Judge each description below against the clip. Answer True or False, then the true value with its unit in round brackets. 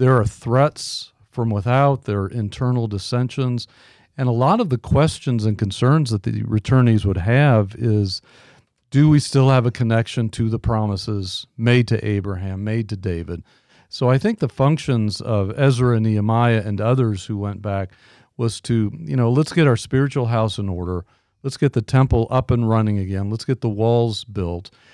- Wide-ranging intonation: False (3.6 semitones)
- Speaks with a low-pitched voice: True (115 Hz)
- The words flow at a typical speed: True (185 wpm)